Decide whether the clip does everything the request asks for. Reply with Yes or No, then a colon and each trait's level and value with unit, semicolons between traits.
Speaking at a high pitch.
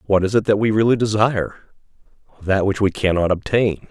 No: low, 100 Hz